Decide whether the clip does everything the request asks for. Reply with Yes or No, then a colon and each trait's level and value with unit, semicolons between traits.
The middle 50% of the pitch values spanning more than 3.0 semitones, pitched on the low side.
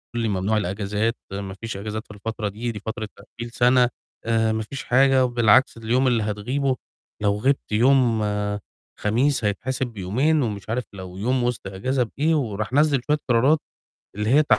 Yes: average, 3.6 semitones; low, 115 Hz